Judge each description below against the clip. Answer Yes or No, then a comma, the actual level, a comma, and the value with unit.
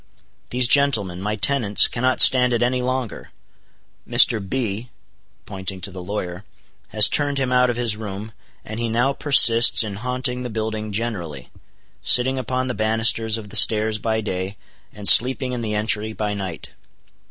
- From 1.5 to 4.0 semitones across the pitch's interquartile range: Yes, average, 3.3 semitones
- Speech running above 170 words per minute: No, average, 165 wpm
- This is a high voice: No, low, 110 Hz